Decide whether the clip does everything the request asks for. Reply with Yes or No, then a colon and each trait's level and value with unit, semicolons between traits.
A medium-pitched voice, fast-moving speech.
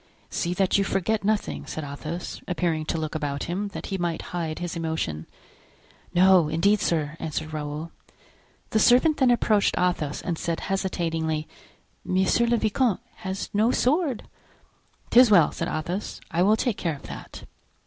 No: medium, 175 Hz; average, 160 wpm